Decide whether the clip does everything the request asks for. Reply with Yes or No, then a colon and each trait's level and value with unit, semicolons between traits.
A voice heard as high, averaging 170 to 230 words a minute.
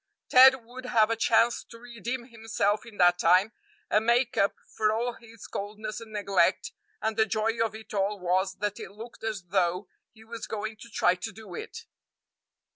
Yes: high, 220 Hz; average, 190 wpm